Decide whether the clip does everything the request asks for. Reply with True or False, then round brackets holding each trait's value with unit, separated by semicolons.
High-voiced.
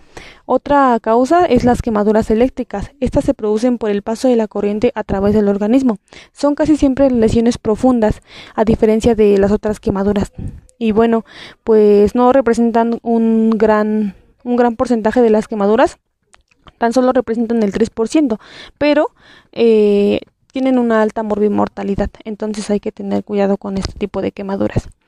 True (225 Hz)